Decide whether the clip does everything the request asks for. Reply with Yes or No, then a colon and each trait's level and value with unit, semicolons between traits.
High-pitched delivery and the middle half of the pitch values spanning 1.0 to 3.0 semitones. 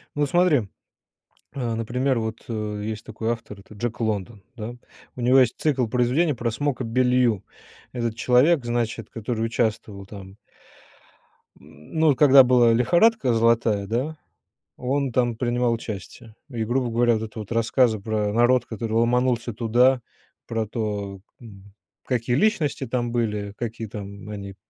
No: low, 115 Hz; narrow, 2.5 semitones